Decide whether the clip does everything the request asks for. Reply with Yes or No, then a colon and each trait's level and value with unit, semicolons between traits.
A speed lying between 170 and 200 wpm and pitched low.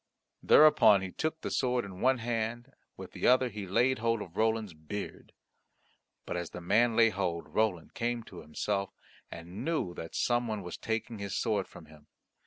Yes: average, 185 wpm; low, 110 Hz